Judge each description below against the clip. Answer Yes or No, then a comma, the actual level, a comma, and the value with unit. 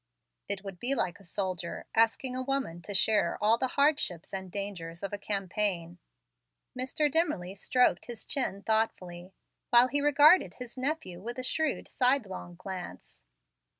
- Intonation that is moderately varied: No, wide, 5.8 semitones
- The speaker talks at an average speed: Yes, average, 150 wpm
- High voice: Yes, high, 210 Hz